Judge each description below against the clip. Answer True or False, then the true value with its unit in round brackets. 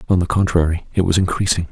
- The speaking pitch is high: False (90 Hz)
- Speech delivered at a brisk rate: True (210 wpm)